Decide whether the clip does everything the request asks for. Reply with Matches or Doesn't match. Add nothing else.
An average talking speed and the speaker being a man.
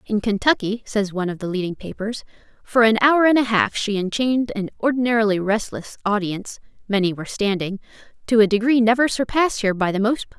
Doesn't match